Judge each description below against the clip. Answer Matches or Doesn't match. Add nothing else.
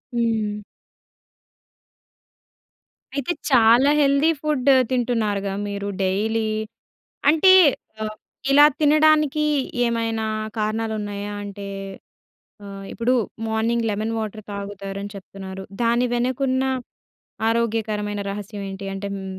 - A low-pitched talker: Doesn't match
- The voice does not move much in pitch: Doesn't match